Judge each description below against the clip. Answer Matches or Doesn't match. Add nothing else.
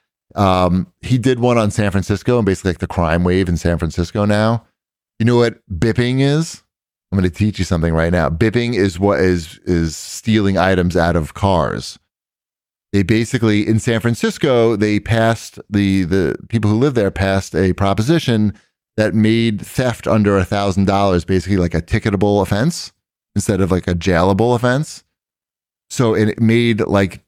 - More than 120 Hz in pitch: Doesn't match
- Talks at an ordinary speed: Matches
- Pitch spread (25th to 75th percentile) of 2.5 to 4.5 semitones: Matches